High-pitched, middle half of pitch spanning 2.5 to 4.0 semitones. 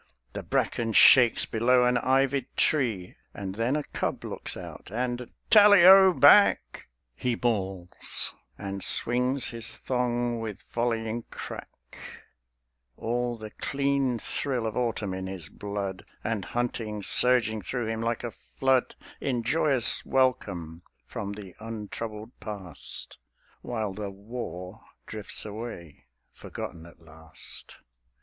No: low, 115 Hz; average, 3.6 semitones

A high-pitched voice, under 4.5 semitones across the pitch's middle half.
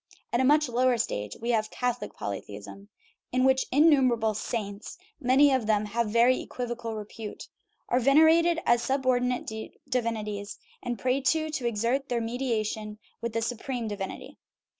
Yes: high, 240 Hz; average, 3.2 semitones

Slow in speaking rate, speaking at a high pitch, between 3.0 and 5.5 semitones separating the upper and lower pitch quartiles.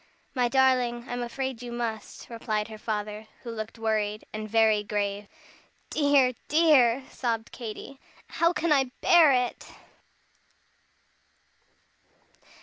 Yes: slow, 115 wpm; high, 235 Hz; average, 3.4 semitones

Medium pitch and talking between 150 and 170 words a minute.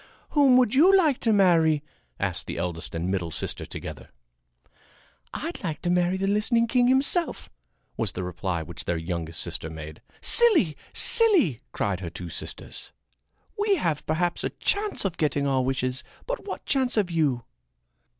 Yes: medium, 165 Hz; average, 165 wpm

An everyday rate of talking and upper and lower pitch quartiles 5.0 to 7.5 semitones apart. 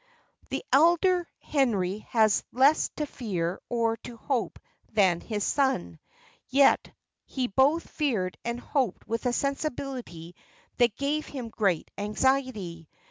No: slow, 125 wpm; wide, 5.5 semitones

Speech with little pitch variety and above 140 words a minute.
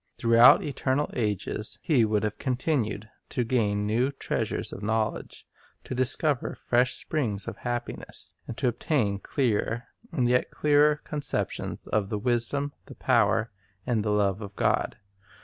No: average, 3.7 semitones; average, 150 wpm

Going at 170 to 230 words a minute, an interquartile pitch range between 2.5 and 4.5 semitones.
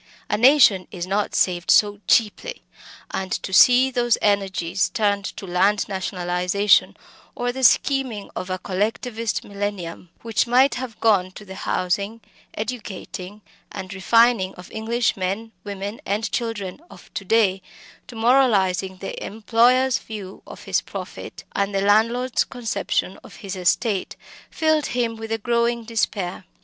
No: average, 140 wpm; average, 3.6 semitones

